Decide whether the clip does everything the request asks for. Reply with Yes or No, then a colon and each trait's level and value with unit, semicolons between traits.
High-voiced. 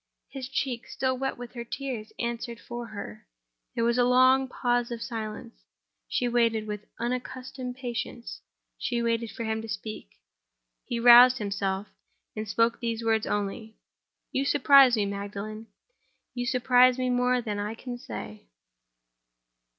Yes: high, 235 Hz